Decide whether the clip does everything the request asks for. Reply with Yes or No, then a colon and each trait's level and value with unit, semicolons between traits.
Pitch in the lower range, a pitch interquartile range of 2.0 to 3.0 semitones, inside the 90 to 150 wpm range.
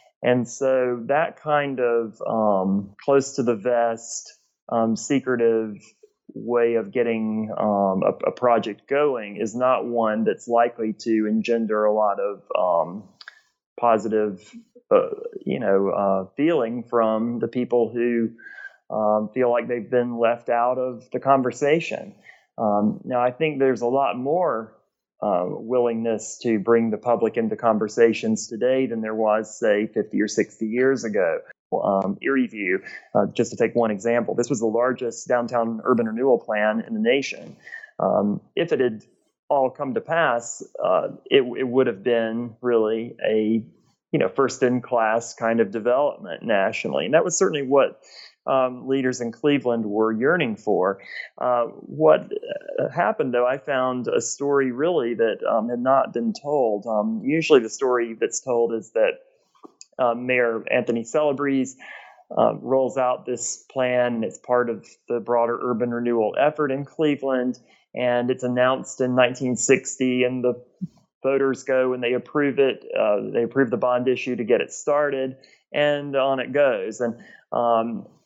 No: low, 125 Hz; narrow, 2.6 semitones; average, 160 wpm